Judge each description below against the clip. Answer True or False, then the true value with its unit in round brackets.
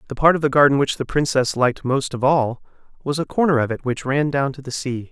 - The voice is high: False (135 Hz)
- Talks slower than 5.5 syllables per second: False (6.0 syllables/s)